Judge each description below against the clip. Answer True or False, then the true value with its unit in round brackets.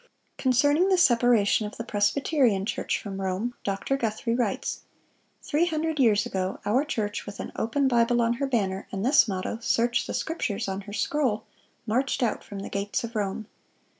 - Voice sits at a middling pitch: False (230 Hz)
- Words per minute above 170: True (180 wpm)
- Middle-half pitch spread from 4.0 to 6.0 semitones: True (4.6 semitones)